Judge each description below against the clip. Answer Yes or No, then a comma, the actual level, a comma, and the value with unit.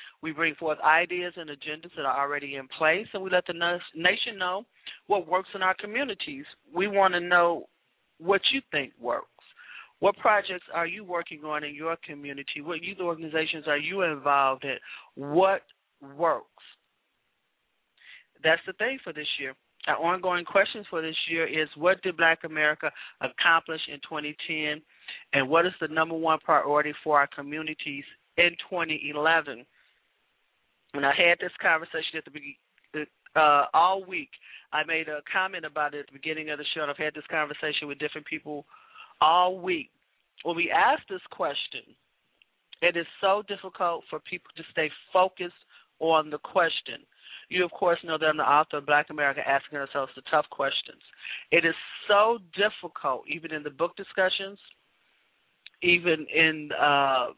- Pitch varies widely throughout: No, average, 3.3 semitones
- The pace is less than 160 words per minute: No, average, 165 wpm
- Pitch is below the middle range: No, medium, 160 Hz